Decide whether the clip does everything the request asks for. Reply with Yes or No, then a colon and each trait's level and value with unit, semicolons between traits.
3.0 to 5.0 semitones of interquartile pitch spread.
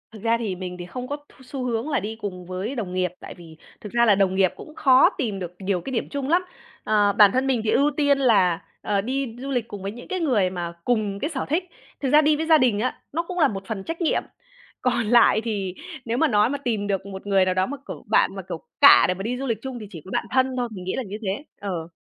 No: wide, 5.4 semitones